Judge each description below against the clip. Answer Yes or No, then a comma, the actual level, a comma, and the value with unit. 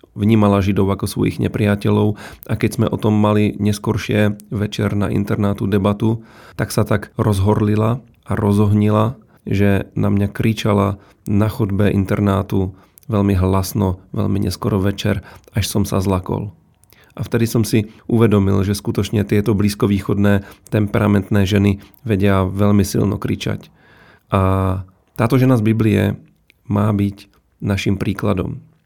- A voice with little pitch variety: Yes, narrow, 1.5 semitones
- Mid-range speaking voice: No, low, 105 Hz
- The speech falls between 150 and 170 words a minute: No, average, 130 wpm